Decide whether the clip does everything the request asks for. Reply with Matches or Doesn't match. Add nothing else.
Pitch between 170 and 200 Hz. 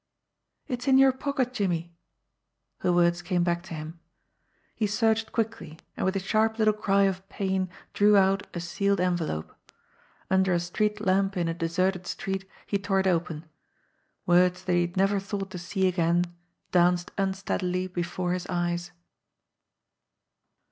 Matches